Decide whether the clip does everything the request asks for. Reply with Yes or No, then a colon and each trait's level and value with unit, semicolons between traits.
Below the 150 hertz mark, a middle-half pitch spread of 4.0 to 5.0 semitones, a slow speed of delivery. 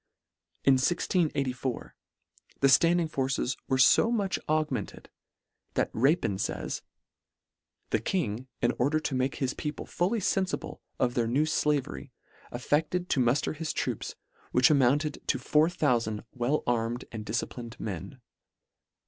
Yes: low, 135 Hz; average, 4.4 semitones; slow, 130 wpm